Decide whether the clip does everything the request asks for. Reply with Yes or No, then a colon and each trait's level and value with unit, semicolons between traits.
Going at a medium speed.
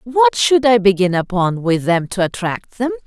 Yes: average, 195 wpm